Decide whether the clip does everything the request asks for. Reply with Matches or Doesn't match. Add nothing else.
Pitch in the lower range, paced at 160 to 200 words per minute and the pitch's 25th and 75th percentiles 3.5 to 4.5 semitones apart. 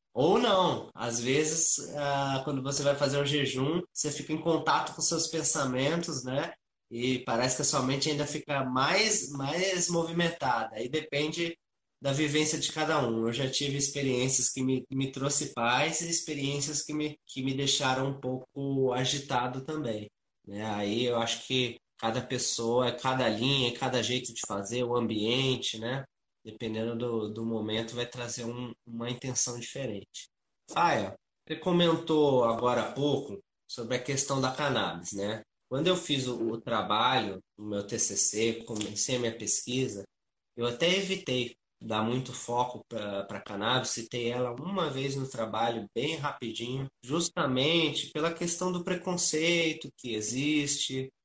Doesn't match